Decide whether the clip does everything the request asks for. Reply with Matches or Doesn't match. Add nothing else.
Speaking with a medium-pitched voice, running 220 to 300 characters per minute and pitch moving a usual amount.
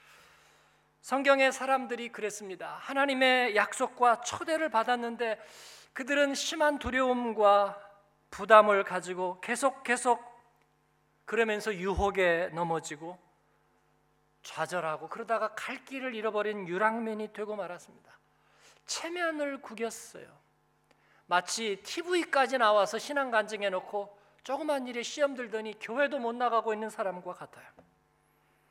Doesn't match